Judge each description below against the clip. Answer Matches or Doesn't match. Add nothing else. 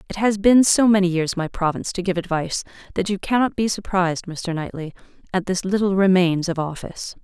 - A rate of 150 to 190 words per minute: Doesn't match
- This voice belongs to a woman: Matches